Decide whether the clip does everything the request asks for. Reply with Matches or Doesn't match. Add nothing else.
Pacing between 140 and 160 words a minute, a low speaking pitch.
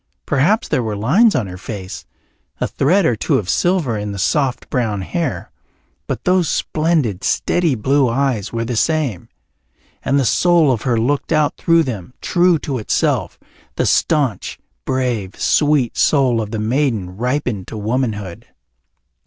Matches